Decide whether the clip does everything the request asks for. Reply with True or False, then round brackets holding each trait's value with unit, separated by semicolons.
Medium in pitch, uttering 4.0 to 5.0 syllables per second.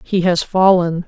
True (180 Hz; 4.1 syllables/s)